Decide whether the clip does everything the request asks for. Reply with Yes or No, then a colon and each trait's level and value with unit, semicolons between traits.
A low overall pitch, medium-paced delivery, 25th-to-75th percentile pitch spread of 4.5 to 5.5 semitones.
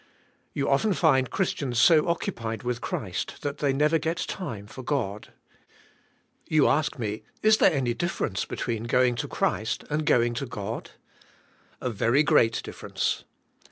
Yes: low, 130 Hz; average, 150 wpm; average, 4.8 semitones